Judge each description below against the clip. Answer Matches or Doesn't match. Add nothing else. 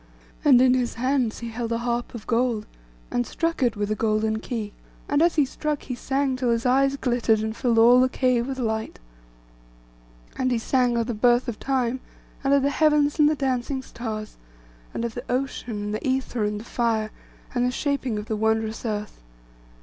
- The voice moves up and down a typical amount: Matches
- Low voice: Doesn't match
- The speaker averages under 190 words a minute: Doesn't match